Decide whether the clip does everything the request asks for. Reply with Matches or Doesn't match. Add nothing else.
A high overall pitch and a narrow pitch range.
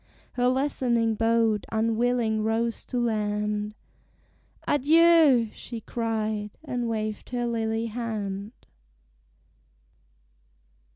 Matches